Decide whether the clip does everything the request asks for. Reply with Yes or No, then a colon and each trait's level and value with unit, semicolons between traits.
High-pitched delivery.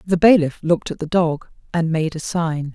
No: medium, 165 Hz